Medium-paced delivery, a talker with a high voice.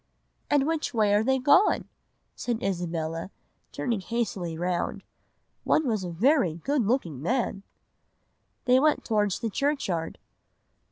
No: slow, 130 wpm; high, 220 Hz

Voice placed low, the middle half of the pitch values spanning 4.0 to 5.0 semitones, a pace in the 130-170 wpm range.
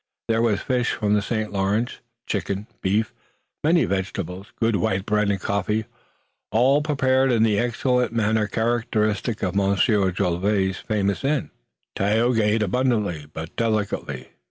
No: low, 105 Hz; average, 3.0 semitones; slow, 135 wpm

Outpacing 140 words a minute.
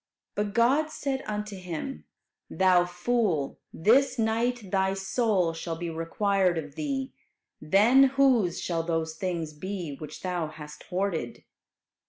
No: slow, 135 wpm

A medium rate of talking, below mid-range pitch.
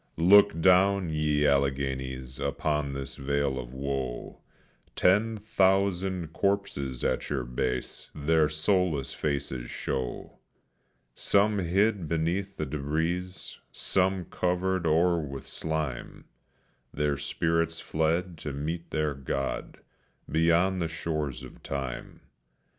No: slow, 110 wpm; very low, 80 Hz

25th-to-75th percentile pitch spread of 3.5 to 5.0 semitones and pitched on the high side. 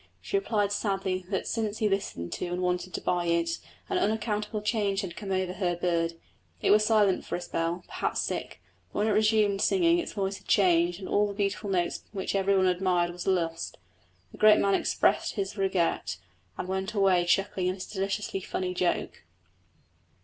No: narrow, 2.6 semitones; high, 195 Hz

